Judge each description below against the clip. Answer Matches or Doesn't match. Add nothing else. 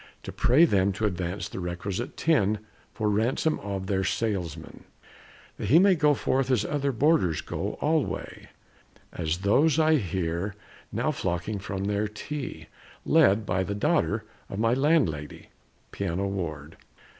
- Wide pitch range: Matches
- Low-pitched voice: Matches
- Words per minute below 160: Matches